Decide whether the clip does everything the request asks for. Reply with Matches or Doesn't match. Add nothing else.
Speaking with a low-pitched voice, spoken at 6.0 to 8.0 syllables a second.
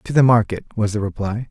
Matches